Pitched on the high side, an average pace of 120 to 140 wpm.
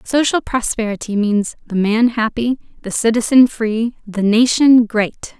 Yes: high, 230 Hz; slow, 135 wpm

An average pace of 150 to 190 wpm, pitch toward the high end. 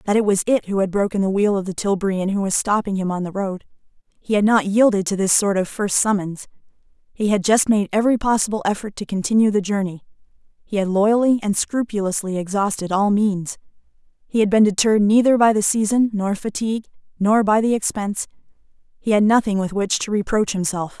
No: fast, 205 wpm; high, 205 Hz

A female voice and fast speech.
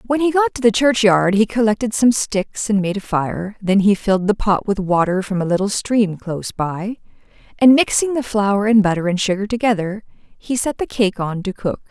Yes: female; fast, 215 wpm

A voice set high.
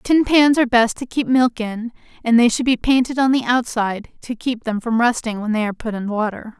Yes: high, 235 Hz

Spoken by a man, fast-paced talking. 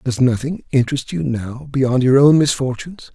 No: male; average, 170 wpm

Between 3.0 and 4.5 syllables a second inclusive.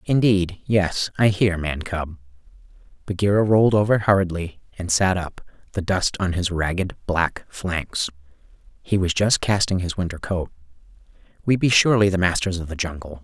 Yes: 4.4 syllables/s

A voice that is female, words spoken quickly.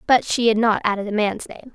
Yes: female; fast, 275 wpm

